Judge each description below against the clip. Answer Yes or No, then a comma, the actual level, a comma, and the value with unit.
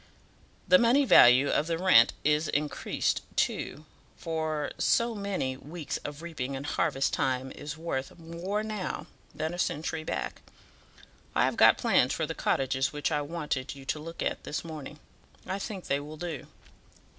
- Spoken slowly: No, average, 165 wpm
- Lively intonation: No, average, 3.2 semitones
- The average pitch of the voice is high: No, medium, 155 Hz